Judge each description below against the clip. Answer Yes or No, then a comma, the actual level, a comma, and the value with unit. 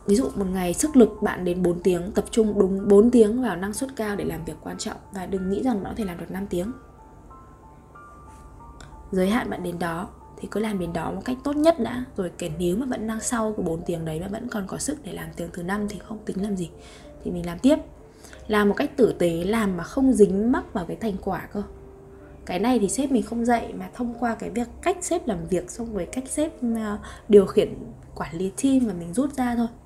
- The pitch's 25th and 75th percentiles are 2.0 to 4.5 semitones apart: Yes, average, 4.2 semitones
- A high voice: Yes, high, 210 Hz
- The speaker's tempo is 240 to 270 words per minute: Yes, fast, 250 wpm